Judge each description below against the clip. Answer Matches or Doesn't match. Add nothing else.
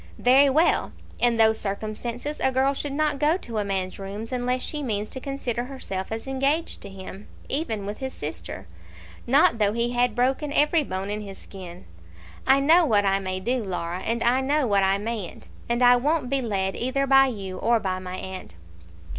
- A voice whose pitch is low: Doesn't match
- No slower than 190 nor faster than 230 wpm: Matches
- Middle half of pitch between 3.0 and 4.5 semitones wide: Doesn't match